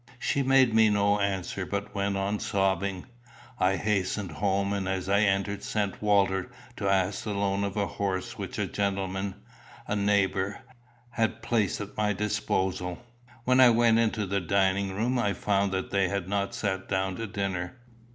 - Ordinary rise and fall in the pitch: No, narrow, 1.5 semitones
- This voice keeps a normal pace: Yes, average, 170 wpm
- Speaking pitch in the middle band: No, low, 100 Hz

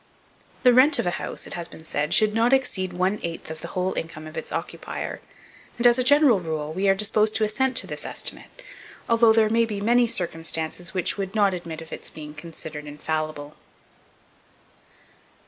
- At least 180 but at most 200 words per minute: Yes, average, 190 wpm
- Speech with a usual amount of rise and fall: No, wide, 5.9 semitones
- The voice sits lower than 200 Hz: Yes, medium, 185 Hz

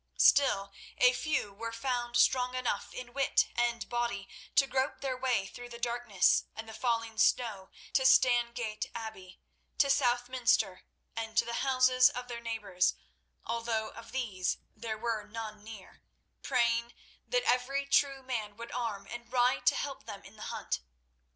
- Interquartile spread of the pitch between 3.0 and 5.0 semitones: No, narrow, 2.4 semitones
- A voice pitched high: Yes, high, 235 Hz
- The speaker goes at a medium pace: Yes, average, 155 wpm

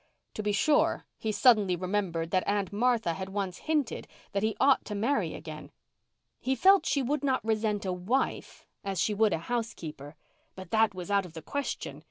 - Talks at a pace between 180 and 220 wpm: Yes, average, 190 wpm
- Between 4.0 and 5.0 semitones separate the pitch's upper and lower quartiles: Yes, average, 4.6 semitones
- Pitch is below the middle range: No, high, 205 Hz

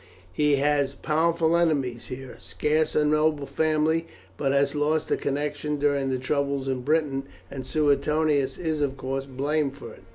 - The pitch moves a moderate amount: No, narrow, 2.1 semitones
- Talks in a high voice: No, medium, 145 Hz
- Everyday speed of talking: Yes, average, 160 wpm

